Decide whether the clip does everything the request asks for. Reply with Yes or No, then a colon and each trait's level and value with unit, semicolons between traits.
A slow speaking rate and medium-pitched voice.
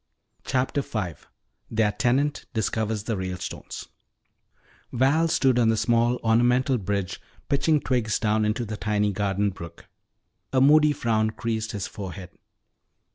No: slow, 130 wpm; low, 110 Hz